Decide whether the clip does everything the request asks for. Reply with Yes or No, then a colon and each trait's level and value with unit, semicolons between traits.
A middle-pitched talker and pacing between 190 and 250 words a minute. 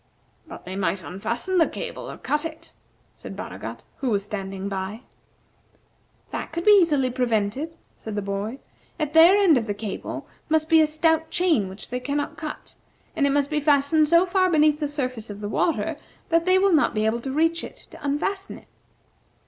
No: very high, 290 Hz; average, 195 wpm